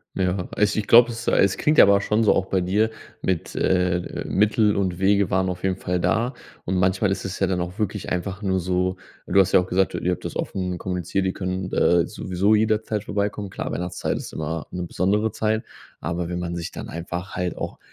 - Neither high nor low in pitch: No, very low, 95 Hz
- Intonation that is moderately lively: No, narrow, 2.2 semitones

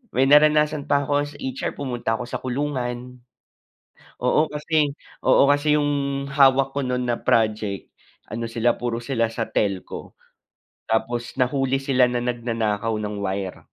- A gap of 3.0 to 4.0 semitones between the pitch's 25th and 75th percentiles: Yes, average, 3.5 semitones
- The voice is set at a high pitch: No, low, 125 Hz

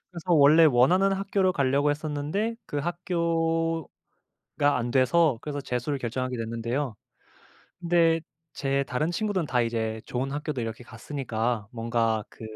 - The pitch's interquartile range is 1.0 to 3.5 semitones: No, average, 5.3 semitones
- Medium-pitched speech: Yes, medium, 145 Hz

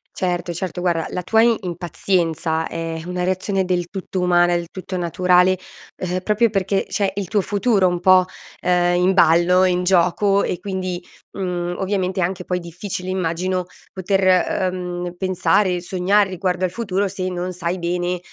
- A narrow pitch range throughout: Yes, narrow, 1.3 semitones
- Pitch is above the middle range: No, medium, 180 Hz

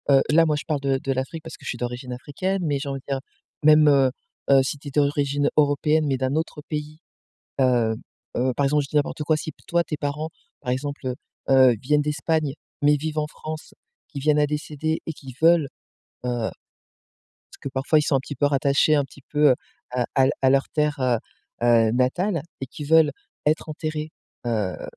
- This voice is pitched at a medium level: Yes, medium, 145 Hz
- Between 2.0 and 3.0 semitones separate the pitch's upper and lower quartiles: Yes, narrow, 2.5 semitones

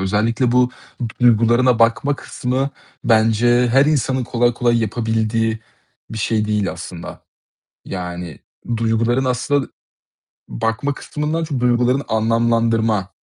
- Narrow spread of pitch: Yes, narrow, 2.2 semitones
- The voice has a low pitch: Yes, low, 115 Hz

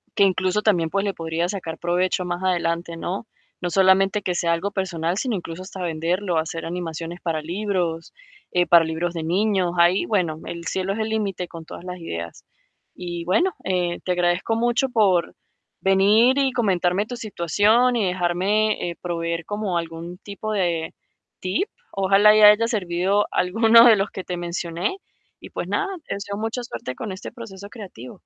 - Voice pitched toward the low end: No, medium, 185 Hz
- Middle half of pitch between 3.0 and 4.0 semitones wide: Yes, average, 3.3 semitones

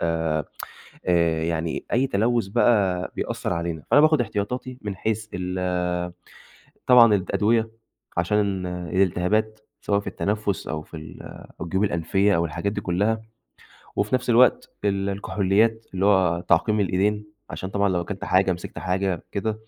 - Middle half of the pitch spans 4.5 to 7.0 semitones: No, average, 3.3 semitones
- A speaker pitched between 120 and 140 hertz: No, low, 100 Hz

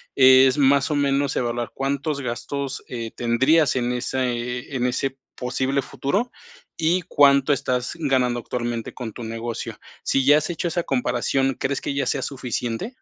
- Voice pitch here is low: Yes, low, 130 Hz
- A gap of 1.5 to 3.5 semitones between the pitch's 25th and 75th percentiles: Yes, narrow, 2.4 semitones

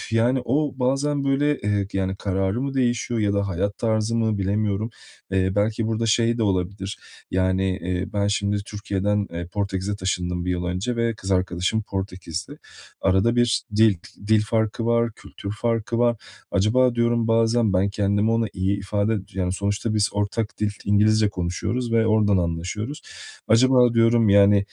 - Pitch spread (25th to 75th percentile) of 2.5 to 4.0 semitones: Yes, average, 3.1 semitones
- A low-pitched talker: Yes, low, 105 Hz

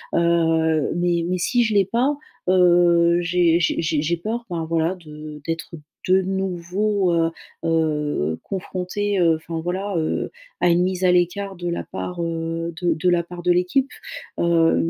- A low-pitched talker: No, medium, 175 Hz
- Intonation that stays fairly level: Yes, narrow, 2.0 semitones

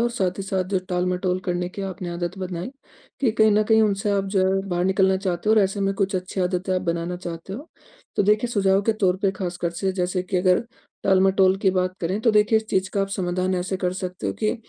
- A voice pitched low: No, high, 190 Hz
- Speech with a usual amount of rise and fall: No, narrow, 1.7 semitones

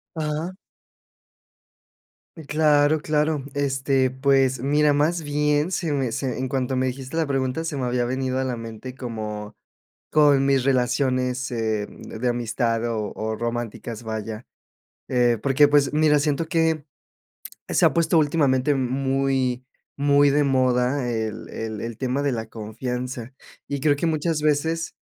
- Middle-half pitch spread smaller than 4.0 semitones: Yes, average, 3.2 semitones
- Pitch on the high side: No, low, 135 Hz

